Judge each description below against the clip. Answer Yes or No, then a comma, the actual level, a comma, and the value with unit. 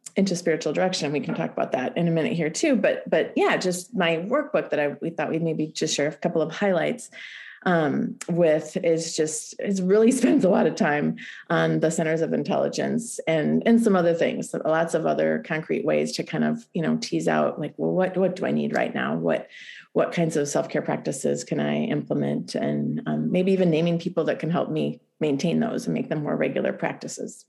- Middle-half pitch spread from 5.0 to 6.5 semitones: No, average, 4.5 semitones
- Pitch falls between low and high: Yes, medium, 165 Hz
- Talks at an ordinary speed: No, fast, 220 wpm